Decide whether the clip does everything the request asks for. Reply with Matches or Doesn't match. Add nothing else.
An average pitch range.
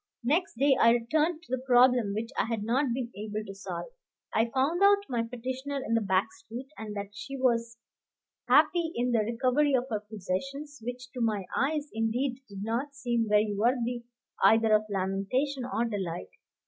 Matches